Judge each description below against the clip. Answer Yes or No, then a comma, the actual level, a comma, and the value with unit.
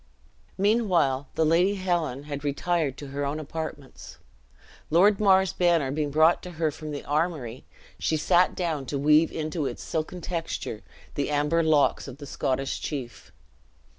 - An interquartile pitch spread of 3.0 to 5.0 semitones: Yes, average, 3.3 semitones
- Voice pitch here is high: No, medium, 155 Hz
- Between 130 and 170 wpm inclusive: Yes, average, 155 wpm